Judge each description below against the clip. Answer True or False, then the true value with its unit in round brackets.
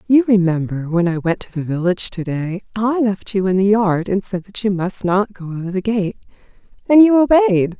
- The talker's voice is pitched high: True (200 Hz)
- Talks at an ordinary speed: False (230 wpm)